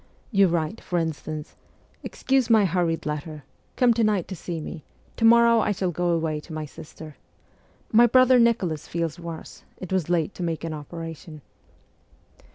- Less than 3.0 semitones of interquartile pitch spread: No, average, 5.1 semitones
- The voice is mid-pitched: Yes, medium, 170 Hz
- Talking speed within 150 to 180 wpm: Yes, average, 170 wpm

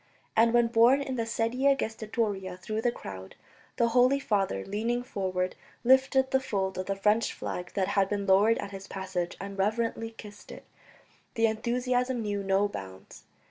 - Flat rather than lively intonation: No, average, 3.5 semitones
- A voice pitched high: Yes, high, 215 Hz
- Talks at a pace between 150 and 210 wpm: Yes, average, 170 wpm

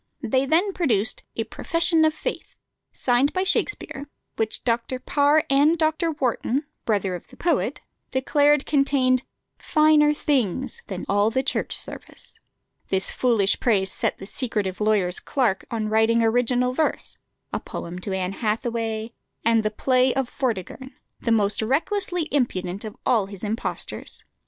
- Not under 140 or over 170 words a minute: Yes, average, 145 wpm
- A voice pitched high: Yes, high, 245 Hz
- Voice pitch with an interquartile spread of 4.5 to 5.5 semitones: Yes, average, 5.0 semitones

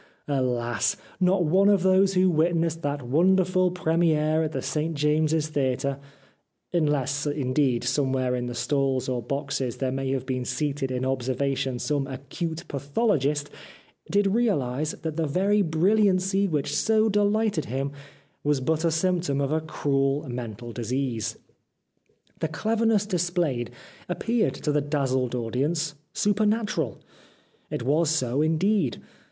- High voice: No, medium, 150 Hz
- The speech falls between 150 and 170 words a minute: No, average, 140 wpm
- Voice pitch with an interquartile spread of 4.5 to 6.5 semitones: Yes, average, 5.2 semitones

